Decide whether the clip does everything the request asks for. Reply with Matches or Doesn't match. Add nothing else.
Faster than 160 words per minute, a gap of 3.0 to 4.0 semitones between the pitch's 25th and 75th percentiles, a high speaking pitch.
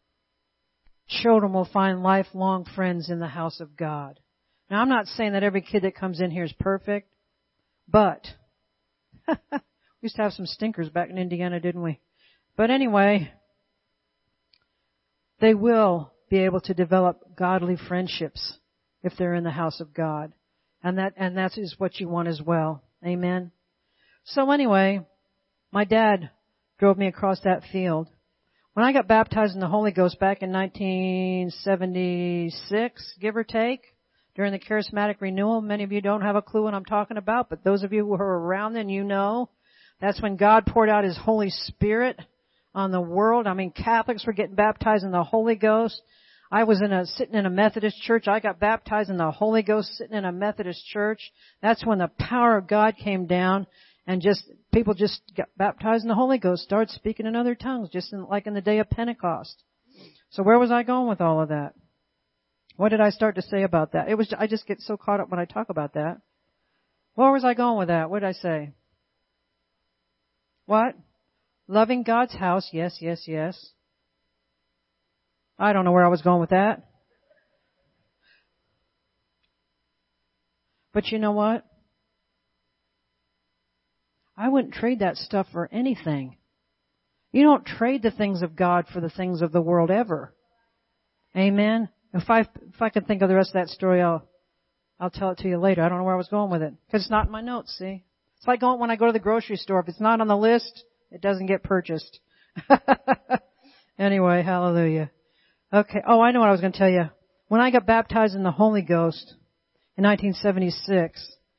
Matches